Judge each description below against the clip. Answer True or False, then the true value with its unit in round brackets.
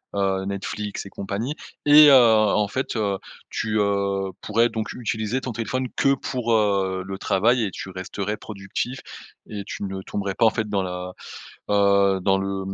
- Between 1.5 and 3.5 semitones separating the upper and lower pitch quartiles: True (2.6 semitones)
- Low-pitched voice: True (100 Hz)